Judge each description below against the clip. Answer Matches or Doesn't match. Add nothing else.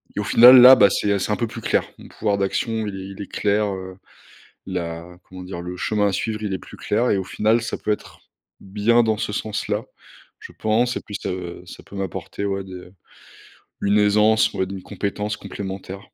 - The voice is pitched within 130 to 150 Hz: Doesn't match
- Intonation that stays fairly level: Matches